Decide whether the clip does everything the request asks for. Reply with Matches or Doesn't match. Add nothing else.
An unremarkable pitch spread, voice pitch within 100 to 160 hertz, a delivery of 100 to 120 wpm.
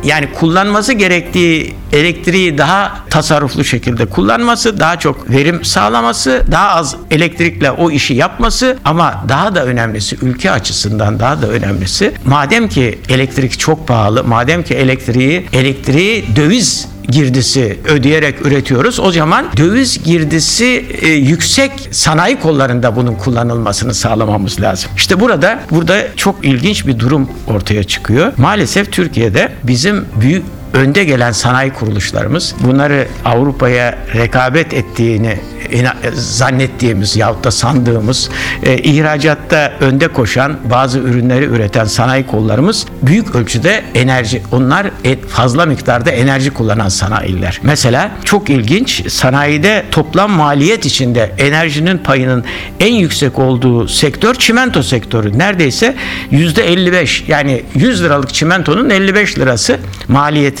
Matches